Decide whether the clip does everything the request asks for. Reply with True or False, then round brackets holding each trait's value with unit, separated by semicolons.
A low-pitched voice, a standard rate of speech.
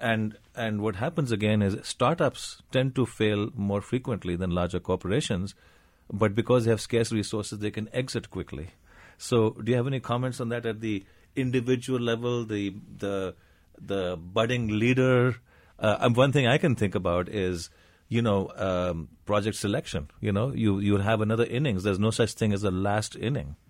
True (105 Hz; 175 wpm)